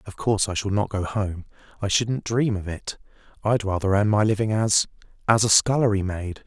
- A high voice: No, low, 105 Hz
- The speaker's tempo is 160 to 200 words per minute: Yes, average, 195 wpm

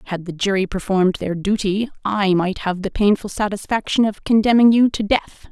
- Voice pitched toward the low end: No, high, 200 Hz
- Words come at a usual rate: Yes, average, 185 wpm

